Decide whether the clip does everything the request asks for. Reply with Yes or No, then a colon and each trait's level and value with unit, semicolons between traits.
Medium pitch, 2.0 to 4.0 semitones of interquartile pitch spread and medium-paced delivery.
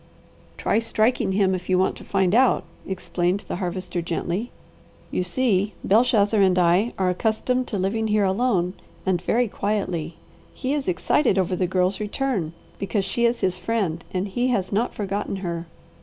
No: high, 195 Hz; average, 3.6 semitones; average, 170 wpm